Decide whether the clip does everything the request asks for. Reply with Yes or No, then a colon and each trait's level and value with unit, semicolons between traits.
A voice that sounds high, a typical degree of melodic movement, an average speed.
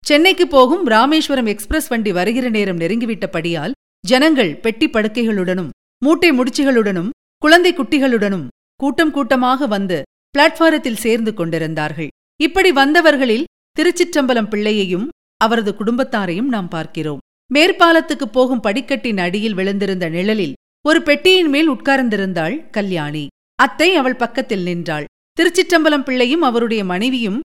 No: high, 245 Hz; wide, 6.7 semitones; average, 105 wpm